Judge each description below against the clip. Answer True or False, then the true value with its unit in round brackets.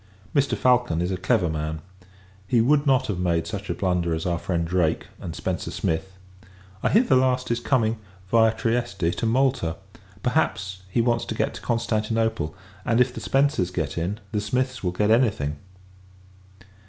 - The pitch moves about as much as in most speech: False (5.9 semitones)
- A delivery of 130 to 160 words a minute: False (180 wpm)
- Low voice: True (105 Hz)